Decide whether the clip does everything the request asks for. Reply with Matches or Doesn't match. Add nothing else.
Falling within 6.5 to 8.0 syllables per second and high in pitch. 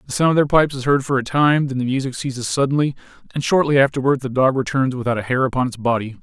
Doesn't match